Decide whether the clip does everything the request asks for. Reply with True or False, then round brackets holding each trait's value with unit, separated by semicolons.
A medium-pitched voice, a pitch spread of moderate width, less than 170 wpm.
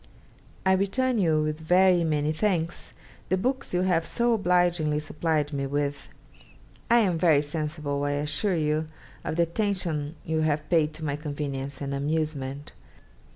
True (155 Hz; 3.4 semitones; 155 wpm)